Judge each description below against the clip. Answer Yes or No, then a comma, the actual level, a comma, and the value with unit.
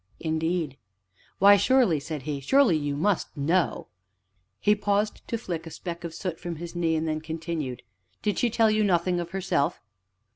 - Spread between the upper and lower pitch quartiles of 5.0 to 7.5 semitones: No, average, 4.3 semitones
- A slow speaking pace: No, average, 180 wpm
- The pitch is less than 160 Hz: No, medium, 170 Hz